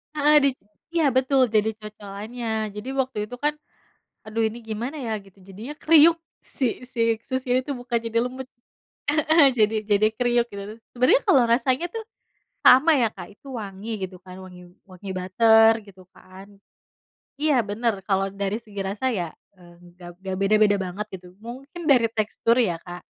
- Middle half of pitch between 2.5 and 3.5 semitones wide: No, average, 4.5 semitones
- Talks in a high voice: Yes, high, 225 Hz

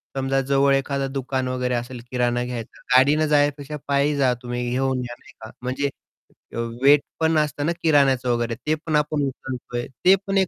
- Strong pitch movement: No, average, 2.7 semitones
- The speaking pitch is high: No, low, 135 Hz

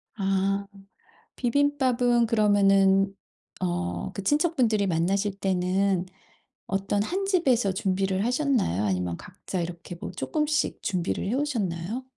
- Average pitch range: Yes, average, 4.8 semitones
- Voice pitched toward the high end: Yes, high, 195 Hz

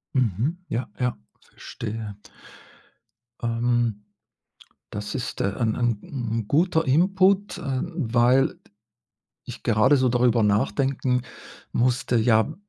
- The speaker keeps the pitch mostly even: No, average, 3.1 semitones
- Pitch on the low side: Yes, low, 120 Hz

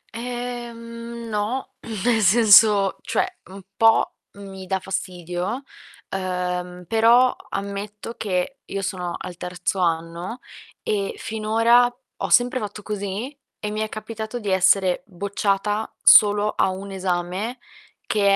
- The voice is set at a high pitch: Yes, high, 205 Hz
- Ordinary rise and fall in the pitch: Yes, average, 3.4 semitones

